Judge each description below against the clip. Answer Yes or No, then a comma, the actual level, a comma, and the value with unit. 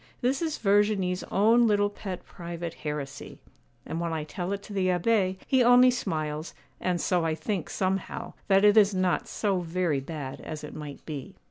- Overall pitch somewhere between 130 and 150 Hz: No, medium, 185 Hz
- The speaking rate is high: No, average, 185 wpm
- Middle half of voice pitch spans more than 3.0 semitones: Yes, average, 4.2 semitones